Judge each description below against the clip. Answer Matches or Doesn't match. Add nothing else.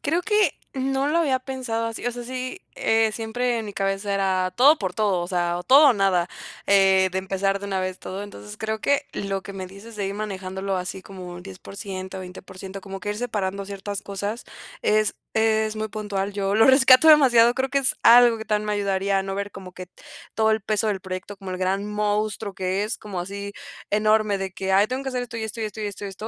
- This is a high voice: Matches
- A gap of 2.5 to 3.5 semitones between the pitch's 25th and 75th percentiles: Matches